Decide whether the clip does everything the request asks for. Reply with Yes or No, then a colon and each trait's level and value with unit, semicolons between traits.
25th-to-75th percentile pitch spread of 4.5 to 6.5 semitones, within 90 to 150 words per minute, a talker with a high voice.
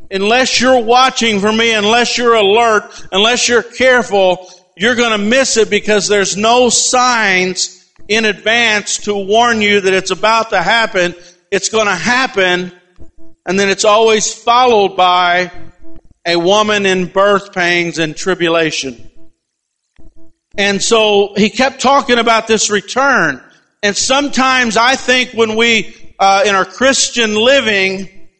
No: average, 4.0 semitones; average, 140 wpm; high, 210 Hz